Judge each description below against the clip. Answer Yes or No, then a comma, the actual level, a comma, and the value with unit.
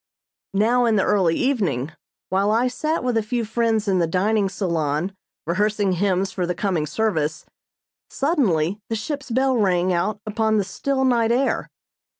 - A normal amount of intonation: Yes, average, 4.3 semitones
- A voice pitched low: No, high, 210 Hz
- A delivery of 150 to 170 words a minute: Yes, average, 160 wpm